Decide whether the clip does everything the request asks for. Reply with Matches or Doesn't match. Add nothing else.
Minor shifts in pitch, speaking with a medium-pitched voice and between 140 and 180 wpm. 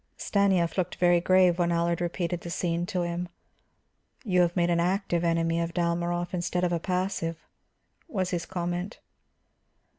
Matches